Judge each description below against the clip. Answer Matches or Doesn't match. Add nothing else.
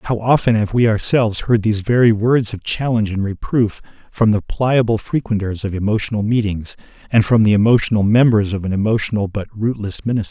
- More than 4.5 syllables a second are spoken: Matches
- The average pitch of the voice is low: Matches